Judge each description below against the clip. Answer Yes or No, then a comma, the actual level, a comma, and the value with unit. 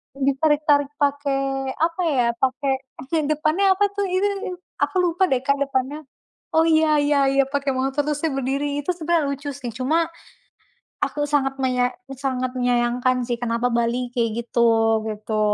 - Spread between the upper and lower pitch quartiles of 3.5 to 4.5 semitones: No, average, 3.1 semitones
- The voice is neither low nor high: No, very high, 275 Hz